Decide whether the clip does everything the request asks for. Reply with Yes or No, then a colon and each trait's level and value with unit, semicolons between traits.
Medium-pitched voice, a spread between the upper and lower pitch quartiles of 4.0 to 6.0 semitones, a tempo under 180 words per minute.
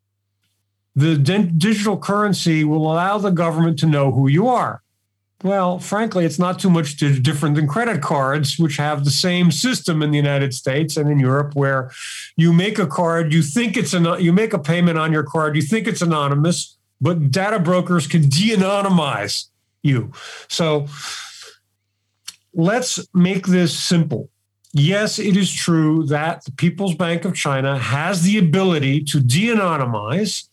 Yes: medium, 165 Hz; average, 4.4 semitones; average, 160 wpm